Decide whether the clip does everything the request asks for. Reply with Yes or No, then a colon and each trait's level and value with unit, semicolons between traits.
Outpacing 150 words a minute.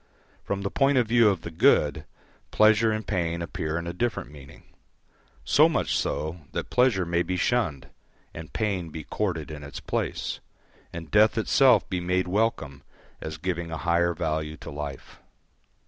Yes: average, 165 wpm